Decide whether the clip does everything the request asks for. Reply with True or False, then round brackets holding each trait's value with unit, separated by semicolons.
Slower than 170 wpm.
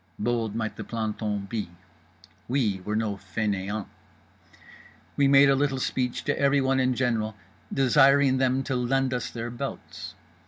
True (145 wpm)